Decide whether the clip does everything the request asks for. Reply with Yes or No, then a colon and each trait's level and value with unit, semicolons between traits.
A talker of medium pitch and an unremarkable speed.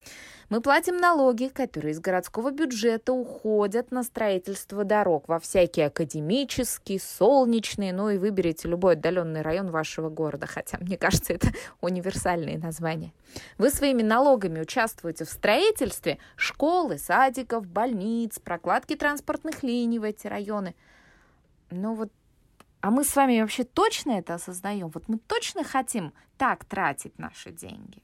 No: high, 215 Hz; average, 135 wpm